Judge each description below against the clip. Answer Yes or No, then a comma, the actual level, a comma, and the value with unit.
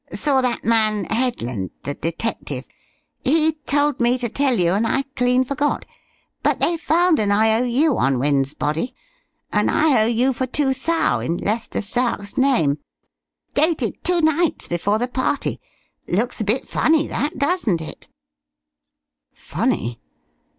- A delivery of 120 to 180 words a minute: Yes, slow, 135 wpm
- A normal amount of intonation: No, wide, 5.9 semitones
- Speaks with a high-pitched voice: Yes, high, 245 Hz